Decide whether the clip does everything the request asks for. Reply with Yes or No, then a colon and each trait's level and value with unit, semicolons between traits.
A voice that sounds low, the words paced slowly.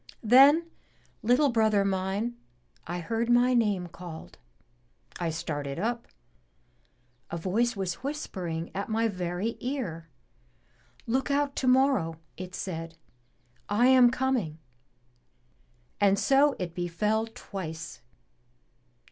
No: high, 210 Hz; slow, 105 wpm